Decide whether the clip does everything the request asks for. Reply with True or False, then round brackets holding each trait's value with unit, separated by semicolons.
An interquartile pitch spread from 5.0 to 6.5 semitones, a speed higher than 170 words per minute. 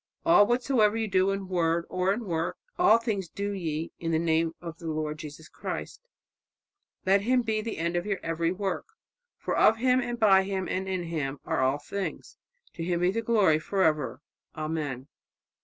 False (4.3 semitones; 190 wpm)